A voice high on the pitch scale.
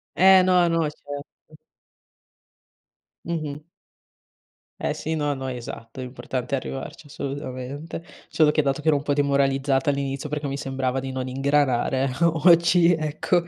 No: medium, 140 Hz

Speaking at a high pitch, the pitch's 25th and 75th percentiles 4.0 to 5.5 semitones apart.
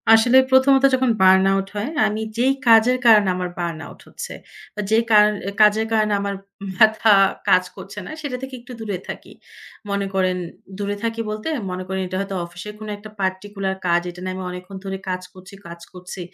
No: high, 200 Hz; average, 3.0 semitones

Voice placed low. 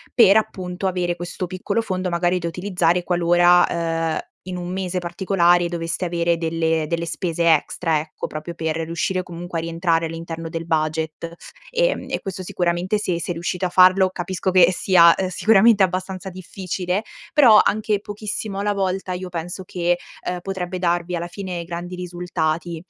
No: medium, 175 Hz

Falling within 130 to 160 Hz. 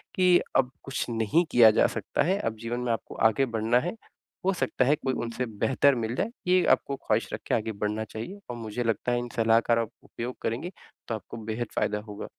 No: low, 120 Hz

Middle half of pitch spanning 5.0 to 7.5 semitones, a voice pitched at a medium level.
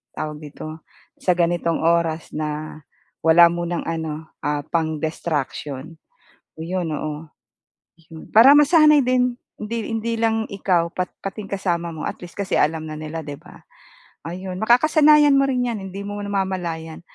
Yes: average, 5.3 semitones; medium, 170 Hz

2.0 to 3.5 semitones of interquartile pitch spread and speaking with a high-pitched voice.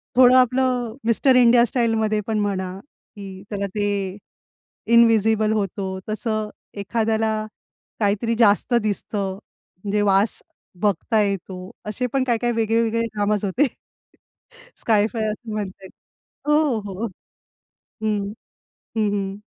Yes: narrow, 2.4 semitones; high, 215 Hz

